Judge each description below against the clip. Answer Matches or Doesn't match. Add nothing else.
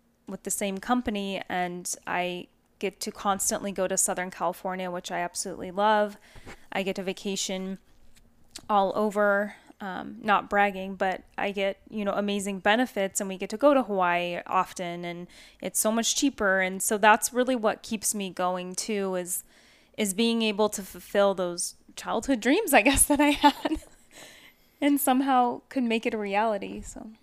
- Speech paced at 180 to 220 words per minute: Doesn't match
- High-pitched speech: Matches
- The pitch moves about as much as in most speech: Matches